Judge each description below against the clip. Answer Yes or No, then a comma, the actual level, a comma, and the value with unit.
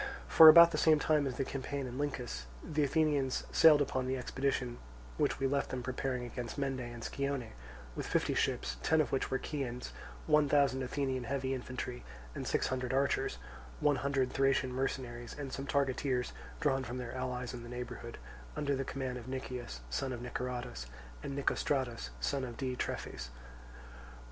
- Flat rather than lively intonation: Yes, narrow, 2.0 semitones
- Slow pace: No, average, 170 wpm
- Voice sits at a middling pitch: No, low, 130 Hz